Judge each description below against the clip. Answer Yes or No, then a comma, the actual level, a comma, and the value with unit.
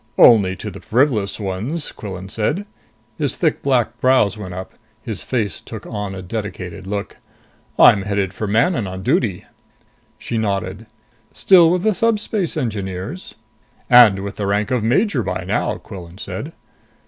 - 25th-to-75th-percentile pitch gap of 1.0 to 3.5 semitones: No, average, 5.0 semitones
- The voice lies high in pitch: No, low, 105 Hz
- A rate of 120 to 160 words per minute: Yes, average, 150 wpm